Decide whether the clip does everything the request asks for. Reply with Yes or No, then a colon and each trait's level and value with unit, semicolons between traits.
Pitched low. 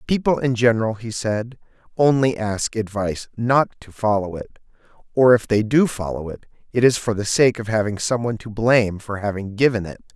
Yes: low, 110 Hz